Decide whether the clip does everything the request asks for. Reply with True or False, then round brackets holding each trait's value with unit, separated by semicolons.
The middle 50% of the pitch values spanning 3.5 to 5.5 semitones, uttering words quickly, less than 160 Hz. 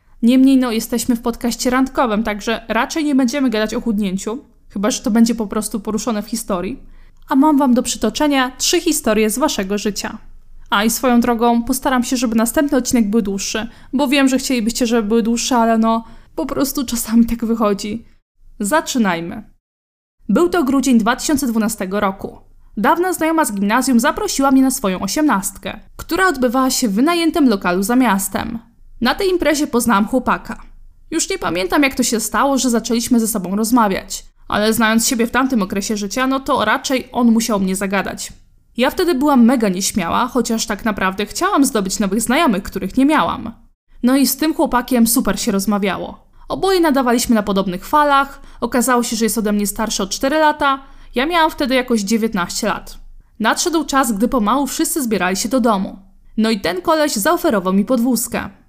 False (3.8 semitones; 175 wpm; 240 Hz)